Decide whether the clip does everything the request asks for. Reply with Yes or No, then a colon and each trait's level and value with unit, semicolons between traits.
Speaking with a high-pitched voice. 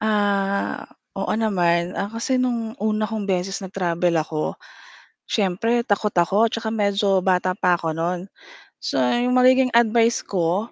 Yes: high, 200 Hz